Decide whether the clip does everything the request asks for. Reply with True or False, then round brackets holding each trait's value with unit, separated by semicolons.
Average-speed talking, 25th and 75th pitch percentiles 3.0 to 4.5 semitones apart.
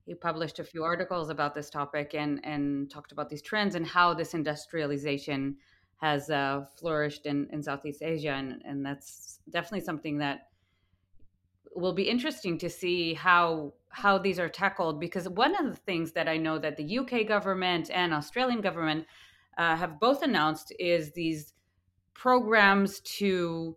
True (160 wpm; 3.6 semitones)